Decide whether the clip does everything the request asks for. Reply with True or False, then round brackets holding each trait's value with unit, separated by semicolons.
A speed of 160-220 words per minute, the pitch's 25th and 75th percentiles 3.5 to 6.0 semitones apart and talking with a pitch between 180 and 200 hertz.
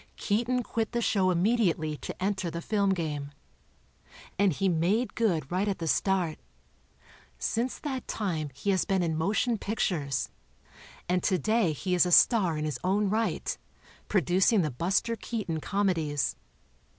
False (150 wpm; 4.6 semitones; 190 Hz)